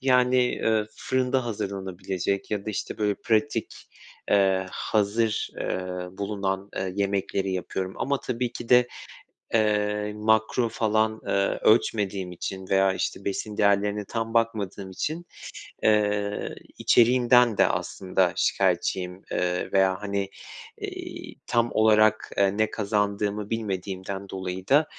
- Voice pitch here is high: No, low, 105 Hz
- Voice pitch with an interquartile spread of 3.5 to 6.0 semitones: No, average, 2.7 semitones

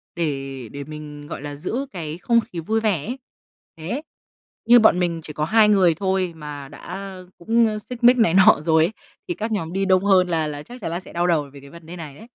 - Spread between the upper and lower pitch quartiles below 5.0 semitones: No, wide, 5.6 semitones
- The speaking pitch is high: No, medium, 175 Hz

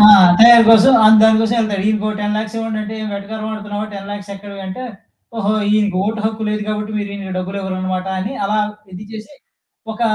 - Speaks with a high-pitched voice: Yes, high, 215 Hz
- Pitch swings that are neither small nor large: No, narrow, 1.6 semitones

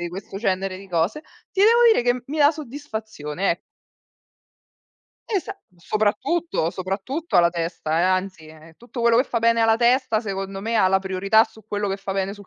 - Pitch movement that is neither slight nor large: Yes, average, 4.3 semitones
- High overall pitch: Yes, high, 205 Hz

